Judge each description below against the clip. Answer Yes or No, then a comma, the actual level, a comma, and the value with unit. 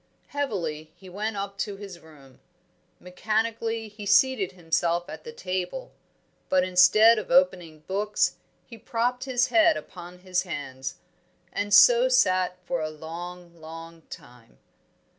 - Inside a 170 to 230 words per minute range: No, slow, 135 wpm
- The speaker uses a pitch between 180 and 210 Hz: Yes, medium, 185 Hz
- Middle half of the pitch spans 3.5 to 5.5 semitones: Yes, average, 4.8 semitones